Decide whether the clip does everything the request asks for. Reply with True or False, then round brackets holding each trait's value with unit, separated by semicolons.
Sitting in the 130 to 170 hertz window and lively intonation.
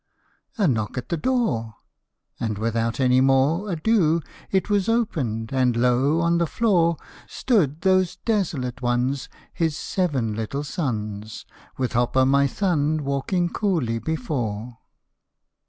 True (140 Hz; 6.1 semitones)